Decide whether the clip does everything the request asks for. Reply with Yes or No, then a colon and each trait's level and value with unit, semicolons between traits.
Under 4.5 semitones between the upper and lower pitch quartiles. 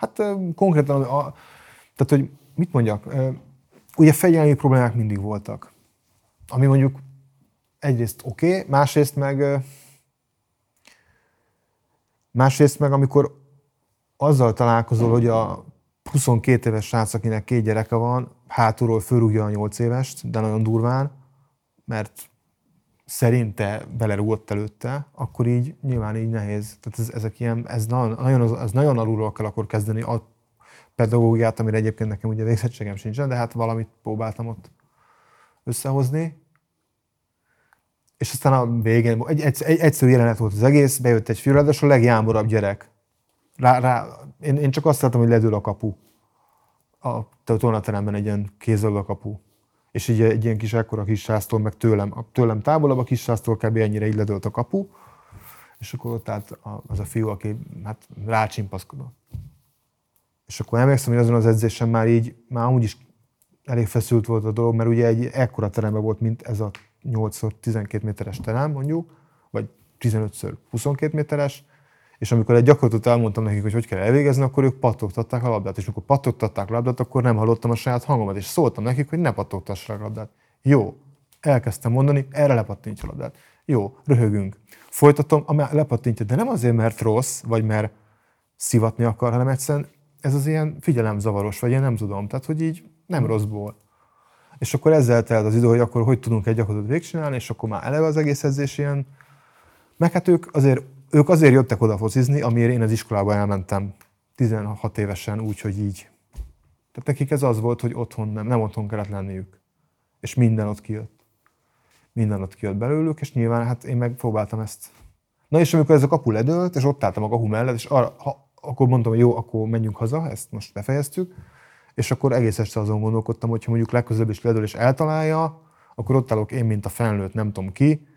Yes: average, 3.8 semitones